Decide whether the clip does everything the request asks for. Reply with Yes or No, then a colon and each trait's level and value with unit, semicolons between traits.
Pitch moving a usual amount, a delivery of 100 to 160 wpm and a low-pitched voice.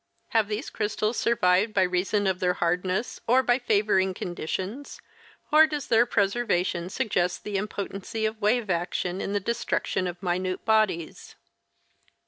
No: average, 3.6 semitones; average, 140 wpm; high, 200 Hz